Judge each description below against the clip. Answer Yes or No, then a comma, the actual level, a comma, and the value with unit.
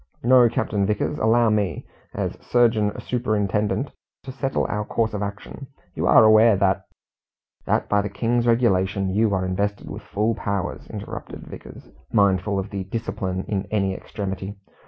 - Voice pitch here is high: No, low, 105 Hz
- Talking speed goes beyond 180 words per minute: No, average, 155 wpm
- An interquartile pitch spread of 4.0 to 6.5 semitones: No, average, 2.7 semitones